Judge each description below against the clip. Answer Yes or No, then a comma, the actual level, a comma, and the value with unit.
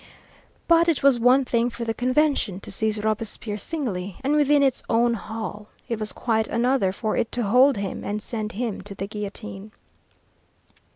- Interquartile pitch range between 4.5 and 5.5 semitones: No, average, 3.4 semitones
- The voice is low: No, high, 225 Hz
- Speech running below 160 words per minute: No, average, 175 wpm